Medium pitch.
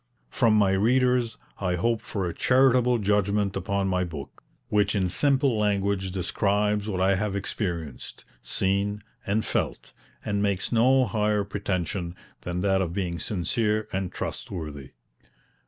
No: low, 100 Hz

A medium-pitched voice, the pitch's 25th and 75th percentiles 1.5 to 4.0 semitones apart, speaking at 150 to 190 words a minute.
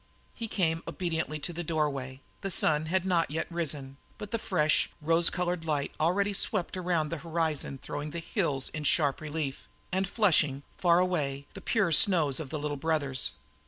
Yes: medium, 160 Hz; average, 3.2 semitones; average, 170 wpm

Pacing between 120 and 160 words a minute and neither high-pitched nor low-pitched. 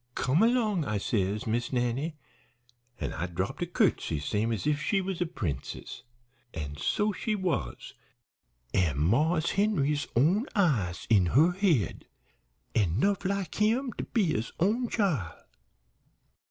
Yes: average, 140 wpm; medium, 150 Hz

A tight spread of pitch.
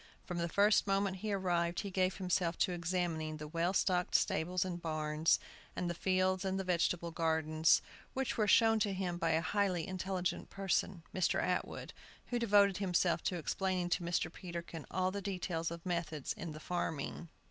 Yes: narrow, 2.3 semitones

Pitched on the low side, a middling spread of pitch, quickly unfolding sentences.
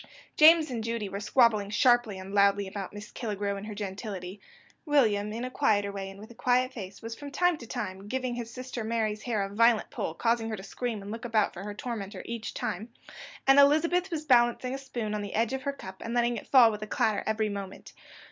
No: high, 225 Hz; average, 3.4 semitones; fast, 235 wpm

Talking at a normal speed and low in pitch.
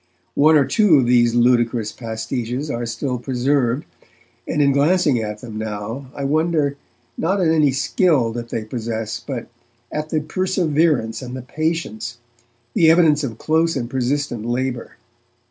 Yes: average, 150 wpm; low, 130 Hz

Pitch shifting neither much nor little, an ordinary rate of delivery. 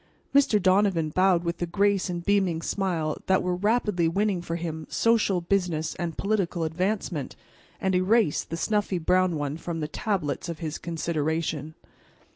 Yes: average, 3.4 semitones; average, 155 wpm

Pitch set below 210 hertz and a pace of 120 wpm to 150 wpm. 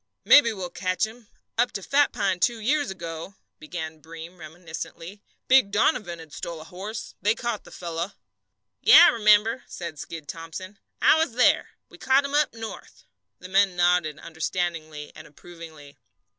No: medium, 185 Hz; average, 160 wpm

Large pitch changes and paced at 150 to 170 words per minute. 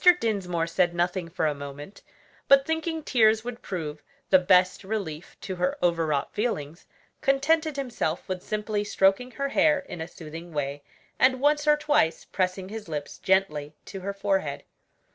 Yes: wide, 6.9 semitones; average, 160 wpm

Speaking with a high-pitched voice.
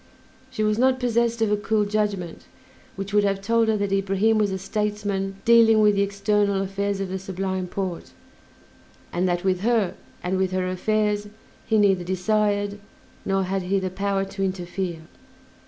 Yes: high, 200 Hz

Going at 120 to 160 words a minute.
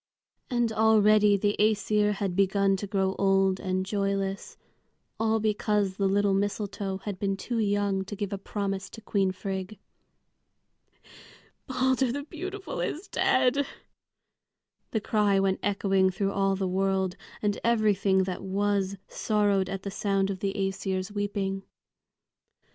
Yes: slow, 135 wpm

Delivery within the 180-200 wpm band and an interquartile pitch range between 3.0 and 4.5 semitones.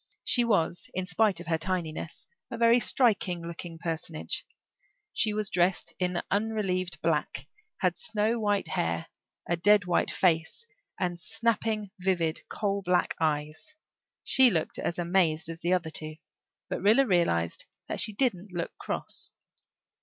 No: average, 145 wpm; average, 4.1 semitones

